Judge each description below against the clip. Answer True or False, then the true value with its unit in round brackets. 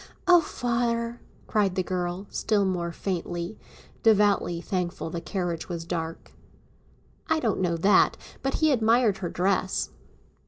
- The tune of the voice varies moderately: True (4.4 semitones)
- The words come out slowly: True (130 wpm)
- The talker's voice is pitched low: False (190 Hz)